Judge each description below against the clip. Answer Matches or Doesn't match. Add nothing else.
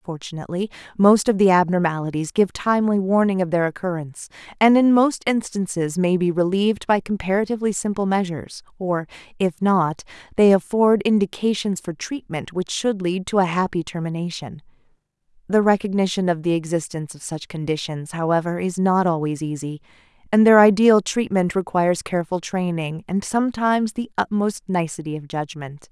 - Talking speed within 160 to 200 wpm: Doesn't match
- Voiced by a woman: Matches